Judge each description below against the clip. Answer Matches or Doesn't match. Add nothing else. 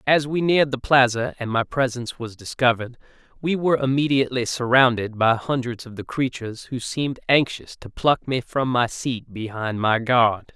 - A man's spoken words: Matches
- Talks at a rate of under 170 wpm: Doesn't match